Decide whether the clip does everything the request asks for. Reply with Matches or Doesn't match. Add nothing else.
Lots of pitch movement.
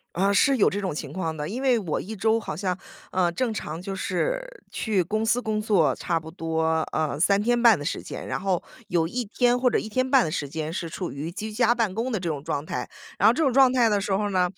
Matches